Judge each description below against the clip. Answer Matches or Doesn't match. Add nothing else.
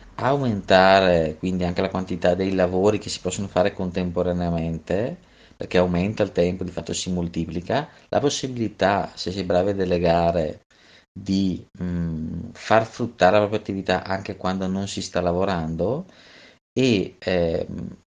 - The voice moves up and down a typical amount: Doesn't match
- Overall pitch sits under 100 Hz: Matches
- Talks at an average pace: Matches